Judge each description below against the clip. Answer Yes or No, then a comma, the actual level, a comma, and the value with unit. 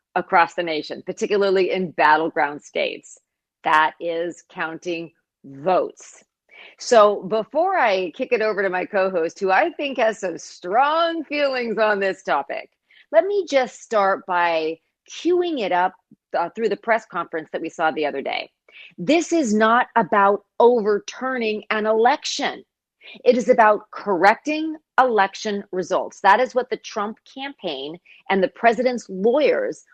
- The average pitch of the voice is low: No, high, 210 Hz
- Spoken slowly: No, average, 145 wpm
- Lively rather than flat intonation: Yes, wide, 6.0 semitones